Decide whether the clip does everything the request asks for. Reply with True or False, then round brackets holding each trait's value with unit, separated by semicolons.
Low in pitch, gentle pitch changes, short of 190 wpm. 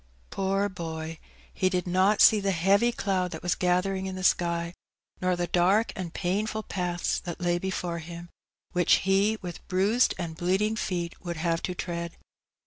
False (180 Hz; 2.0 semitones; 170 wpm)